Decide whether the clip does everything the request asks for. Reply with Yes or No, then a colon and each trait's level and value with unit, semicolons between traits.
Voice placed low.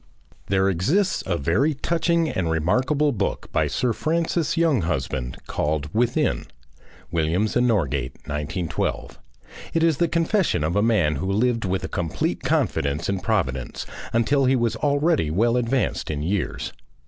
Yes: low, 105 Hz